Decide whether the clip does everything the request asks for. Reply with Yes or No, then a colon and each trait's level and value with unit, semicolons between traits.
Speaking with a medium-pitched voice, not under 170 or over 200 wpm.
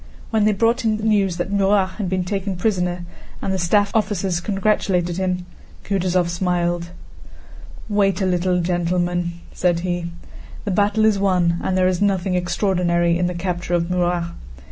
No: medium, 180 Hz; average, 160 wpm